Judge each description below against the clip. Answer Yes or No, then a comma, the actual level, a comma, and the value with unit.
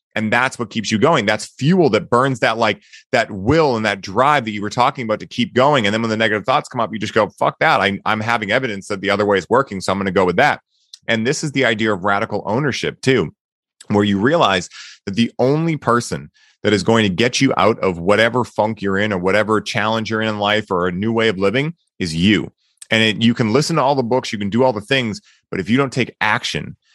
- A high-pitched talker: No, low, 110 Hz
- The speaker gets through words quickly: Yes, fast, 265 wpm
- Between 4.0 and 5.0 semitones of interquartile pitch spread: No, average, 2.8 semitones